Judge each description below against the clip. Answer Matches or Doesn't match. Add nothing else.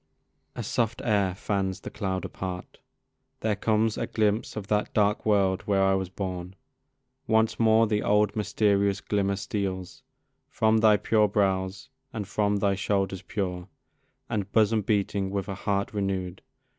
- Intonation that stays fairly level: Matches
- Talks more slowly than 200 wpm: Matches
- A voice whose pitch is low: Matches